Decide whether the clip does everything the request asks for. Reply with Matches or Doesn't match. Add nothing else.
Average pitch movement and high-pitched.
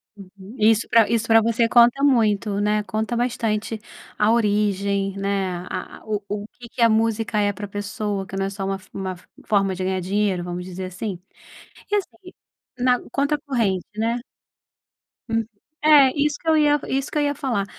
Matches